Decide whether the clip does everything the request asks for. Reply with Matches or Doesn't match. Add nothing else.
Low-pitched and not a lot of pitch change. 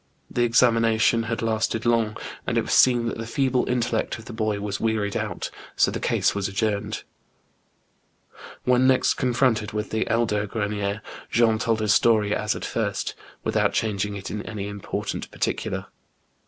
Matches